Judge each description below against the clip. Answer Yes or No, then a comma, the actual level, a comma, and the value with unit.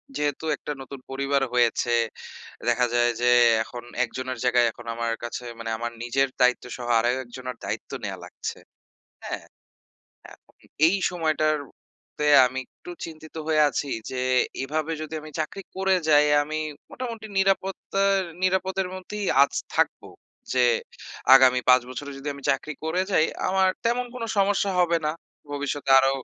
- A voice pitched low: No, medium, 145 Hz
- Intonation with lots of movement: Yes, wide, 6.2 semitones